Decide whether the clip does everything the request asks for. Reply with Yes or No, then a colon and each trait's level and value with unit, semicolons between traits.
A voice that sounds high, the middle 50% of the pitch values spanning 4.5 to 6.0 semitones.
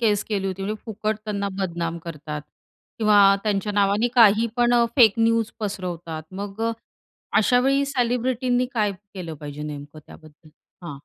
Yes: high, 205 Hz; average, 5.1 semitones